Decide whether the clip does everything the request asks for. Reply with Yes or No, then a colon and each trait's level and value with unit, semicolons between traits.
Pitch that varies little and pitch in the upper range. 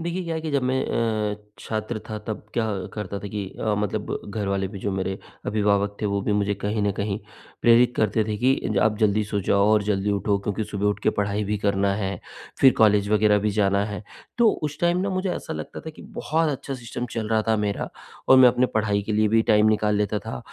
No: narrow, 2.1 semitones; low, 105 Hz